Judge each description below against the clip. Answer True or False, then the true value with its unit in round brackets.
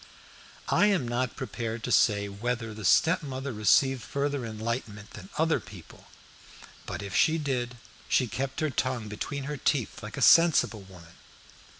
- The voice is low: True (125 Hz)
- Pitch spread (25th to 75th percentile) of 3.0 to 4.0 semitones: False (4.7 semitones)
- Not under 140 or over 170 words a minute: True (155 wpm)